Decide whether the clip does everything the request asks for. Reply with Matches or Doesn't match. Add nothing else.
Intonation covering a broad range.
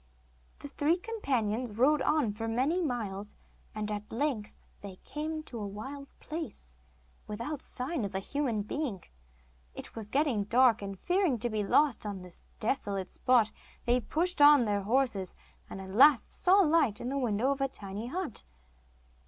Matches